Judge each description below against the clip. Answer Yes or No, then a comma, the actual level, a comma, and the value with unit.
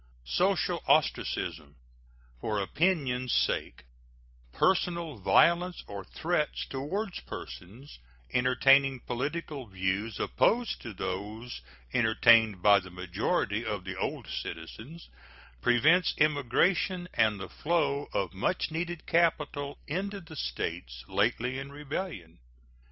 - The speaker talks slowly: Yes, slow, 105 wpm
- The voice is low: Yes, low, 130 Hz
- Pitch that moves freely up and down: Yes, wide, 8.3 semitones